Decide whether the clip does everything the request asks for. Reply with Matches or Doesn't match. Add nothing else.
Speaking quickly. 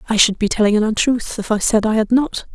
Matches